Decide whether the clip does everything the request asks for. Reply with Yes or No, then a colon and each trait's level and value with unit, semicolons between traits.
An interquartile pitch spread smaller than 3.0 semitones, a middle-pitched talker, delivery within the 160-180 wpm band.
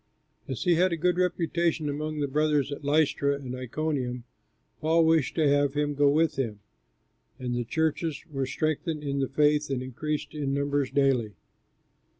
Yes: narrow, 2.4 semitones; medium, 145 Hz; average, 165 wpm